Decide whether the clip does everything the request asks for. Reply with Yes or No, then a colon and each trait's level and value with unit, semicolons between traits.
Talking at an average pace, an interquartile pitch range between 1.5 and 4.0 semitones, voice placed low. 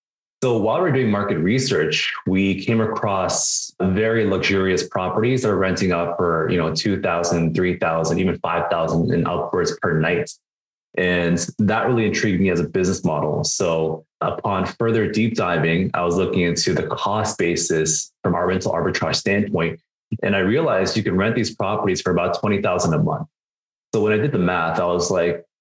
Yes: average, 185 wpm; average, 3.7 semitones; very low, 90 Hz